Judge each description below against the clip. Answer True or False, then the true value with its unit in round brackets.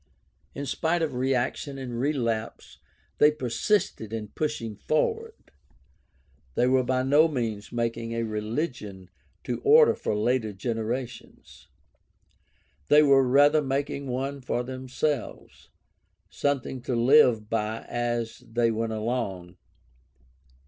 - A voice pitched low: True (125 Hz)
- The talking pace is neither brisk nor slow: False (115 wpm)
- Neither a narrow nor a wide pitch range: True (3.8 semitones)